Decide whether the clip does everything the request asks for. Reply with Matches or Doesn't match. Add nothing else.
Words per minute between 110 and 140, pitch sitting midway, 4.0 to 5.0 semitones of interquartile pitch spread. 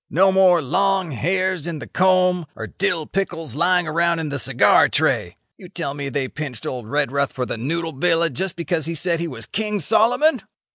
Doesn't match